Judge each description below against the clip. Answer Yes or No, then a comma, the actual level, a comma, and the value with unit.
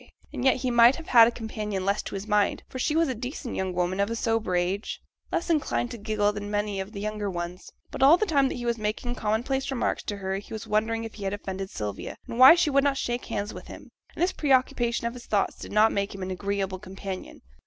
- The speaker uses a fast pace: Yes, fast, 260 wpm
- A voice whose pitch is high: Yes, high, 215 Hz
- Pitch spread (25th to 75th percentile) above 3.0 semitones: Yes, average, 3.8 semitones